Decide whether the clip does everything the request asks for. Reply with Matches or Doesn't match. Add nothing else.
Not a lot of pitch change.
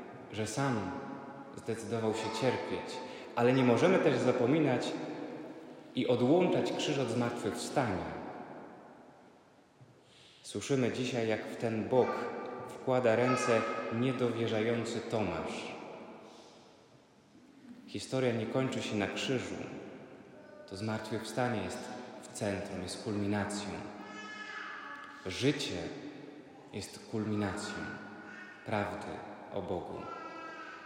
Doesn't match